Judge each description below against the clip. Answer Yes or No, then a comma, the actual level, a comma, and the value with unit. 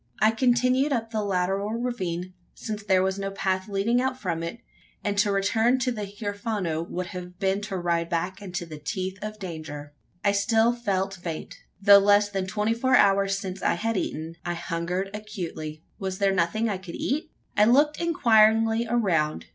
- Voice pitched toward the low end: No, high, 200 Hz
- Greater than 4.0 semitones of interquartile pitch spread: No, average, 3.6 semitones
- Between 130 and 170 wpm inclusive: No, average, 180 wpm